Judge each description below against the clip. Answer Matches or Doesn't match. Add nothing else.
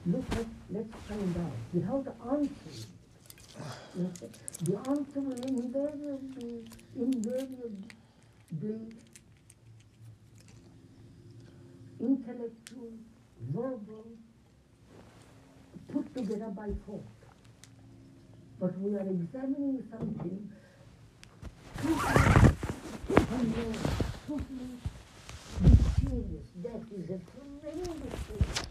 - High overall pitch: Matches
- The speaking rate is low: Matches